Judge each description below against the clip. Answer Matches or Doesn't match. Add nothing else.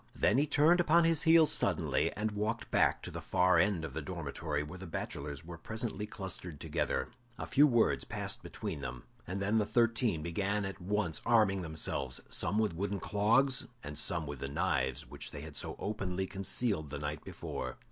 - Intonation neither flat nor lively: Doesn't match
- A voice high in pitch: Doesn't match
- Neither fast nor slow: Matches